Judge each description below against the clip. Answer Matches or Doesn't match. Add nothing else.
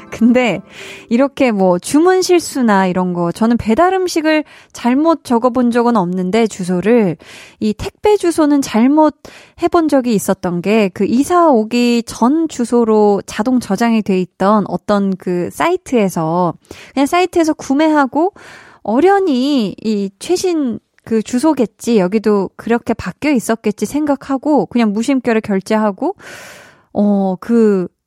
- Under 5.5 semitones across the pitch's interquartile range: Doesn't match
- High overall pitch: Matches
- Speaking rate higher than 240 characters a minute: Matches